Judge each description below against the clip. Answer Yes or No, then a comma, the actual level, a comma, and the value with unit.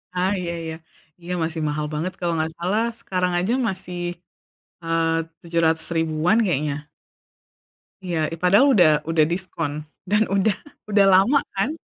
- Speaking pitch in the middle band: Yes, medium, 175 Hz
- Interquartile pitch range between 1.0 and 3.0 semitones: Yes, average, 2.7 semitones